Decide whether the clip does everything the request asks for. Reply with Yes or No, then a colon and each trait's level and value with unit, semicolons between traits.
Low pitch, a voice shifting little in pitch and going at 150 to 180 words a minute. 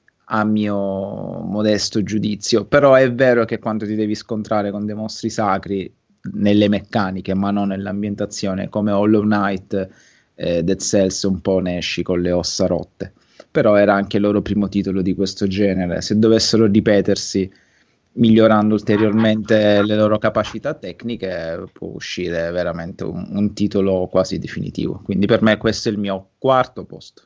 Yes: low, 105 Hz; narrow, 2.0 semitones; average, 155 wpm